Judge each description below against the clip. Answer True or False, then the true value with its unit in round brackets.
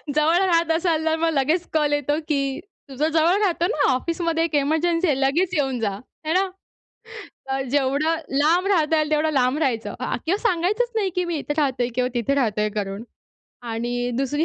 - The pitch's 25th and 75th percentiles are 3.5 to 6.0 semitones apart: True (3.8 semitones)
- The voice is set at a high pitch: True (305 Hz)